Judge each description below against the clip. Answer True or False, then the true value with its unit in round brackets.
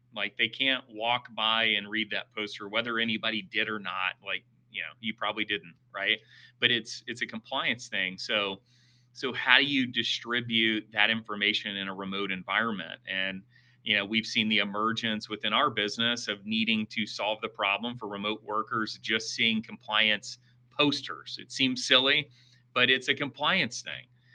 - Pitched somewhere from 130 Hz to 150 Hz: False (115 Hz)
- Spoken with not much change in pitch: False (3.1 semitones)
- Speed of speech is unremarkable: True (175 wpm)